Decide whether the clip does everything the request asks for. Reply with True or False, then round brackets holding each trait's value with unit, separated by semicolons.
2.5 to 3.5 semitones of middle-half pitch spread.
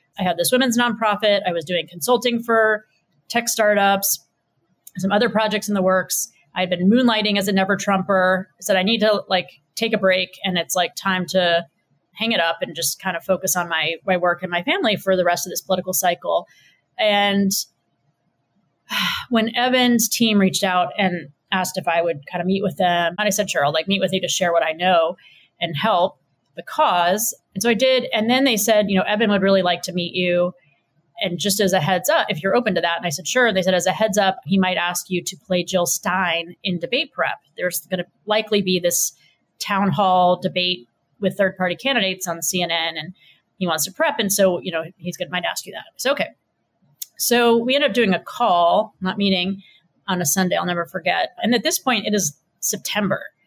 True (3.1 semitones)